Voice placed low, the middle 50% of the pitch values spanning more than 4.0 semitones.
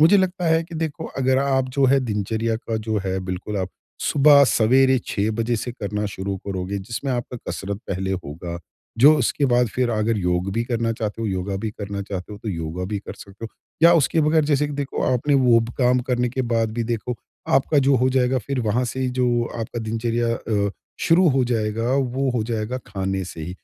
Yes: low, 115 Hz; average, 4.4 semitones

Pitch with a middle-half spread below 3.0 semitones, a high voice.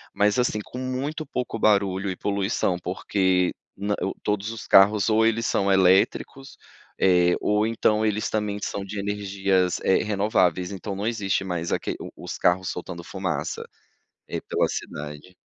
No: narrow, 2.5 semitones; low, 100 Hz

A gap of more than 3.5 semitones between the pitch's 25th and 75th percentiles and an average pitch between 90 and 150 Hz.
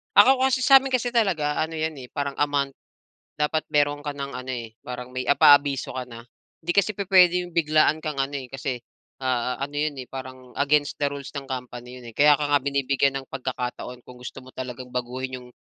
No: average, 3.2 semitones; medium, 140 Hz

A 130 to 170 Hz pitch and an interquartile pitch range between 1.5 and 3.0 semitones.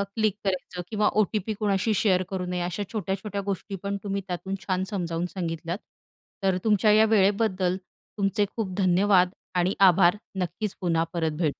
No: high, 190 Hz; narrow, 2.4 semitones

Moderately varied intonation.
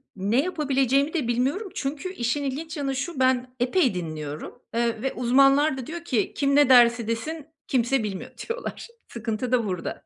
Yes: average, 3.5 semitones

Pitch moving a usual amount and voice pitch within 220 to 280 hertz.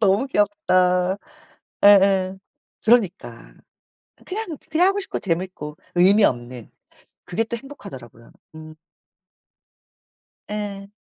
No: average, 4.8 semitones; high, 195 Hz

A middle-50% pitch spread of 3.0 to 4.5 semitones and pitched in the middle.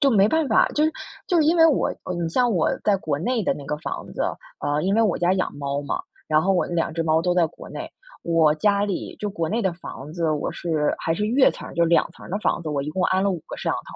No: average, 4.9 semitones; medium, 175 Hz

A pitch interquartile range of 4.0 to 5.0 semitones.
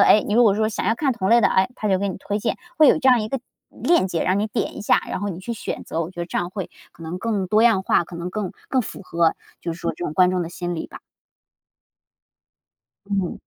No: average, 3.6 semitones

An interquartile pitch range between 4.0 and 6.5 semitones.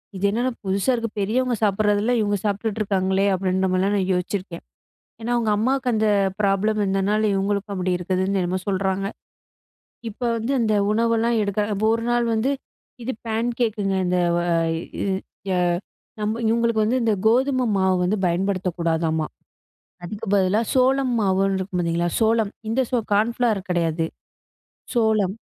No: average, 3.2 semitones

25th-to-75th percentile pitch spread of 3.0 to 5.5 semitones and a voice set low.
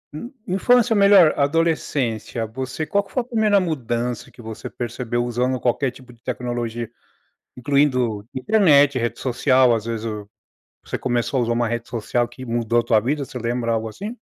Yes: average, 3.9 semitones; low, 125 Hz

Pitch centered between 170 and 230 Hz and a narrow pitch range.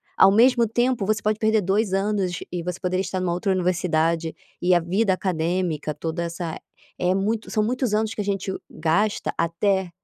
No: high, 190 Hz; average, 3.6 semitones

